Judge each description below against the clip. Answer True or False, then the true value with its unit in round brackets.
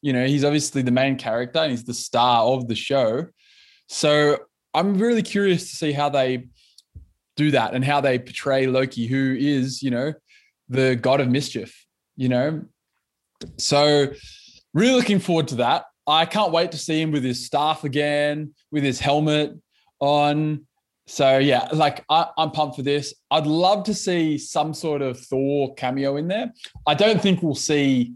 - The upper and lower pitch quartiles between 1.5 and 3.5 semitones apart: True (3.1 semitones)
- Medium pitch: True (145 Hz)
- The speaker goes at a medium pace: True (175 wpm)